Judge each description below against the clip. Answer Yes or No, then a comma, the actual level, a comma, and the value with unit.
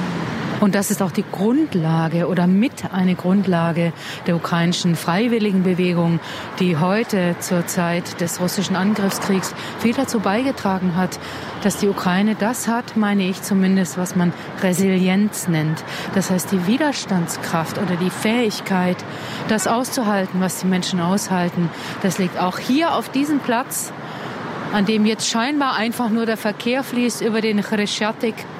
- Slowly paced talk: No, average, 145 wpm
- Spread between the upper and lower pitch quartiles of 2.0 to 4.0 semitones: Yes, average, 3.5 semitones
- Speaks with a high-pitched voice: Yes, high, 195 Hz